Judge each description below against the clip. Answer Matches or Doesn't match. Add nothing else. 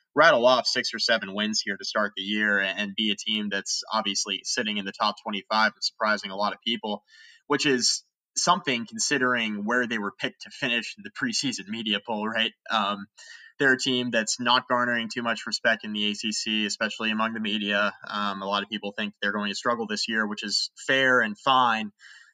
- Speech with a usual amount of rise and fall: Doesn't match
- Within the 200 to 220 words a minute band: Matches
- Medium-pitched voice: Doesn't match